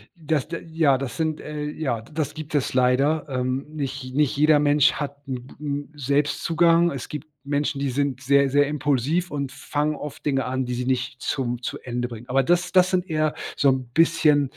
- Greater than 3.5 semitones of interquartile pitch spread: No, average, 2.7 semitones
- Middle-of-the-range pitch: Yes, medium, 145 Hz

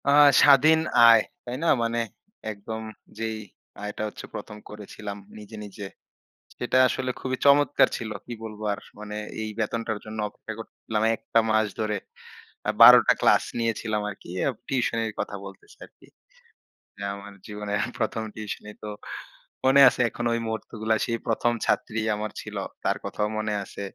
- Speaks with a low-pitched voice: Yes, low, 110 Hz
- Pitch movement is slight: Yes, narrow, 1.8 semitones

